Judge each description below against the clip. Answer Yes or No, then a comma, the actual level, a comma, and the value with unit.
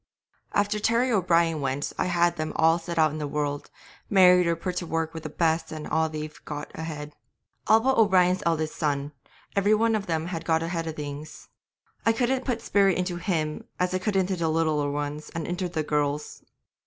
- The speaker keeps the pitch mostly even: No, average, 3.3 semitones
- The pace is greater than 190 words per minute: Yes, fast, 205 wpm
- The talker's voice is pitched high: No, medium, 165 Hz